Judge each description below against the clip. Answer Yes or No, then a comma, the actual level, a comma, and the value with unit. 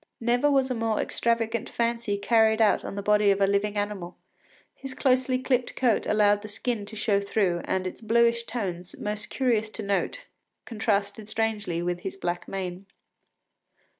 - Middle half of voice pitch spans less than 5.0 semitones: Yes, average, 2.7 semitones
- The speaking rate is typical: Yes, average, 165 wpm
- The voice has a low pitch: No, high, 215 Hz